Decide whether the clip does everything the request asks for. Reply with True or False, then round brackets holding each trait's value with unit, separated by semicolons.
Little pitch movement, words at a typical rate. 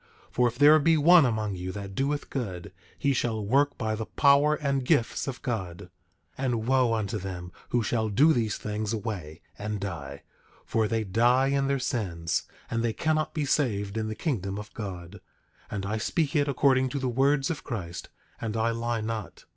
False (5.0 semitones; 195 wpm)